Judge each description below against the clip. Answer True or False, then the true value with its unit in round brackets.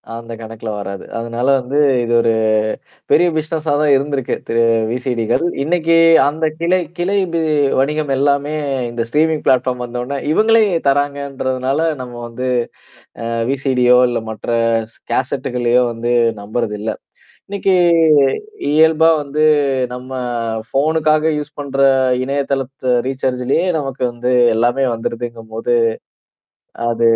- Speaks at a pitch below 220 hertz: True (135 Hz)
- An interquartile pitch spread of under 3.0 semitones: False (3.8 semitones)